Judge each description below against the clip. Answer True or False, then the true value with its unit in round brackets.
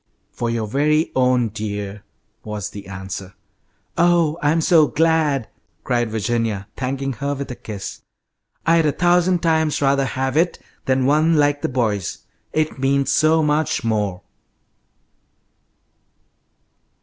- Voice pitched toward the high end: False (135 Hz)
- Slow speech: True (125 wpm)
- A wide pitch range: True (5.8 semitones)